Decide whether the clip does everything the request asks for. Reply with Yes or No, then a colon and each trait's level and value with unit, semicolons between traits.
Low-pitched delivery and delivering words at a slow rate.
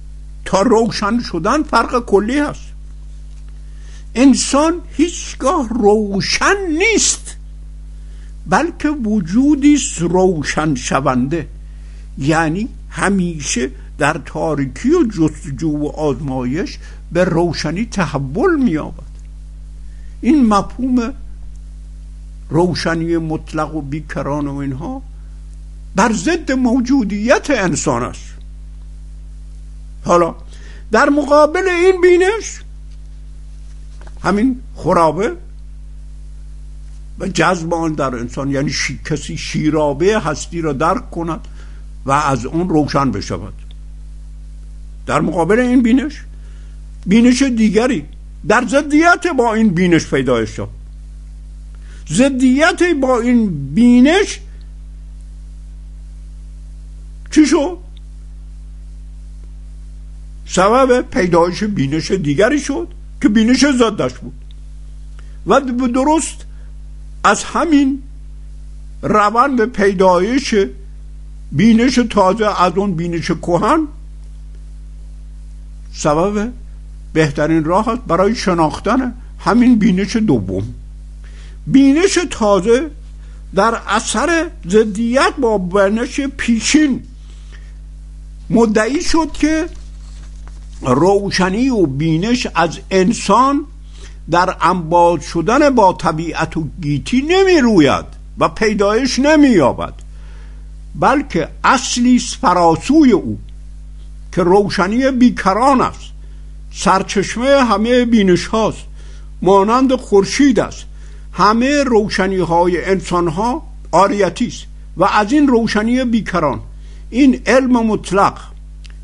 No: medium, 175 Hz; slow, 85 wpm